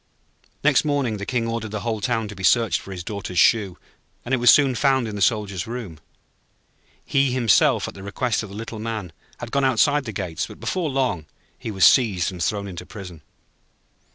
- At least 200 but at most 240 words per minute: Yes, fast, 205 wpm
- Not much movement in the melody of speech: No, average, 4.3 semitones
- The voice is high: No, low, 110 Hz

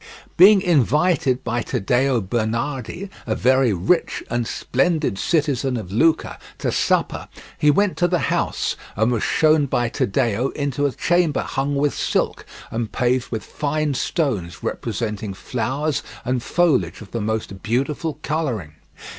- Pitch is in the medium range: No, low, 130 Hz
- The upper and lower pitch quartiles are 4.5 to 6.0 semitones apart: Yes, average, 5.1 semitones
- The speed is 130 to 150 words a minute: Yes, average, 140 wpm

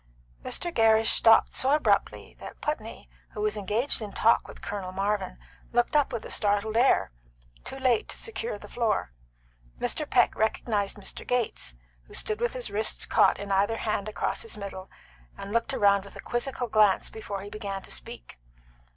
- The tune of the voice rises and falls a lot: No, average, 2.8 semitones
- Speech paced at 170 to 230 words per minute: Yes, average, 175 wpm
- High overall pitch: Yes, high, 215 Hz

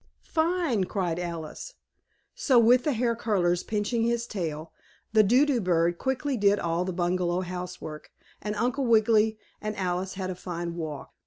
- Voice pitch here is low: No, high, 200 Hz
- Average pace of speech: Yes, average, 160 wpm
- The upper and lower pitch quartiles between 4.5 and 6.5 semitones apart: Yes, average, 5.2 semitones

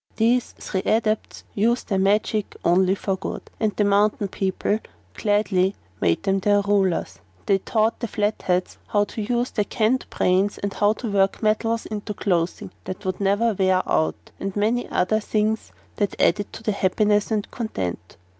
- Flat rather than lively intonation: Yes, narrow, 2.1 semitones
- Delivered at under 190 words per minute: Yes, average, 165 wpm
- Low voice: No, high, 205 Hz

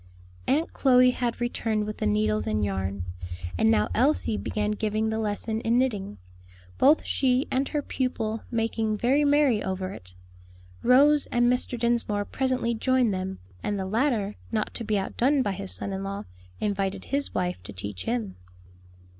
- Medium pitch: No, high, 220 Hz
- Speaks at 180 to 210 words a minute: No, average, 165 wpm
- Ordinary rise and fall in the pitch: Yes, average, 4.6 semitones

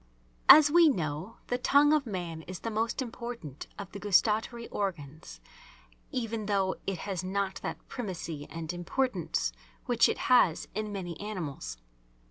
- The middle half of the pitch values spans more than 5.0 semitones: Yes, wide, 5.5 semitones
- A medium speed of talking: Yes, average, 145 wpm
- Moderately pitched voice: No, high, 200 Hz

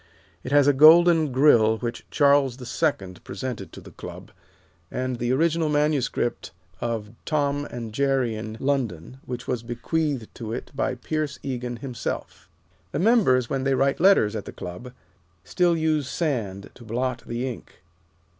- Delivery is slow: No, average, 155 wpm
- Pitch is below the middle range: Yes, low, 130 Hz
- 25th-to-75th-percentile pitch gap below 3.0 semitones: No, average, 3.8 semitones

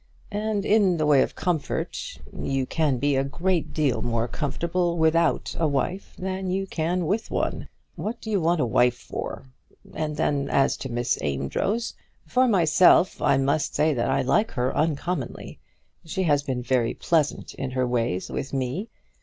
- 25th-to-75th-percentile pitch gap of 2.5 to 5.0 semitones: No, wide, 5.4 semitones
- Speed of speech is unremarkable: Yes, average, 170 wpm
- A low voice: No, medium, 155 Hz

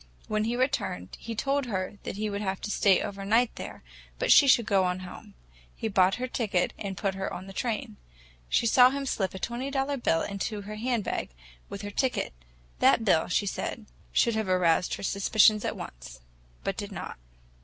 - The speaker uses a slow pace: No, average, 195 wpm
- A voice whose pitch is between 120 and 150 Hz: No, high, 205 Hz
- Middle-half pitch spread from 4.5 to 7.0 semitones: No, average, 3.9 semitones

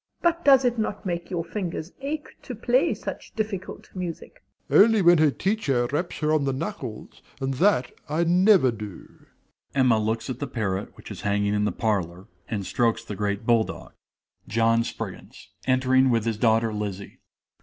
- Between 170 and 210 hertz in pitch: No, low, 130 Hz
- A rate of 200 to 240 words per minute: No, average, 175 wpm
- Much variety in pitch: Yes, wide, 8.4 semitones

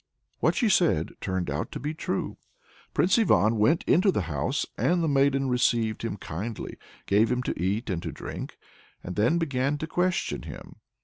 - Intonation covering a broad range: Yes, wide, 7.8 semitones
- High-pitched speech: No, low, 125 Hz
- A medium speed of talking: Yes, average, 180 wpm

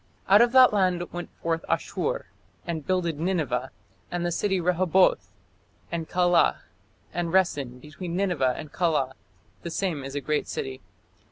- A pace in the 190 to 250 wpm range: No, average, 150 wpm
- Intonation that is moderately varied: Yes, average, 3.6 semitones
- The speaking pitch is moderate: Yes, medium, 170 Hz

